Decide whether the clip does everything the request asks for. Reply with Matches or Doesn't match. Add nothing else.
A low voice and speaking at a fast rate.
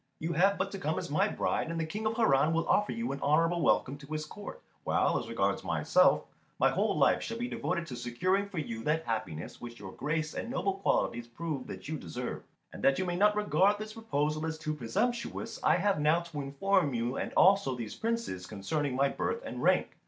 Doesn't match